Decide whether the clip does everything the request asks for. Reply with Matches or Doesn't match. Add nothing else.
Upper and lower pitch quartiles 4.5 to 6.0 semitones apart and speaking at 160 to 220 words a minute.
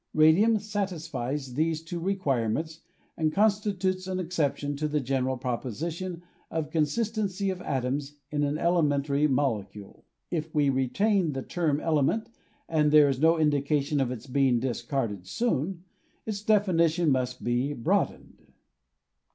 Doesn't match